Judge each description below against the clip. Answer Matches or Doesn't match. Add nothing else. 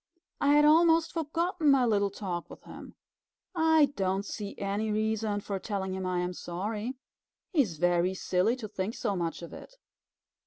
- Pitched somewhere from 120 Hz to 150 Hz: Doesn't match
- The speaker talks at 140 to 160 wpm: Doesn't match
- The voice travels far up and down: Matches